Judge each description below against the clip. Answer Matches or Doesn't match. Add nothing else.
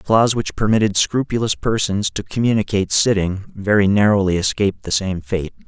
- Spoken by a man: Matches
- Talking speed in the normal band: Matches